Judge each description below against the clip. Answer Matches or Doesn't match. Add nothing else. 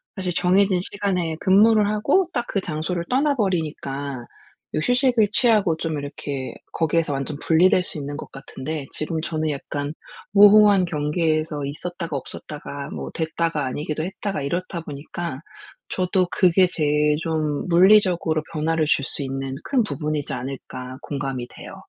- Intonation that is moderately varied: Matches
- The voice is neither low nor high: Matches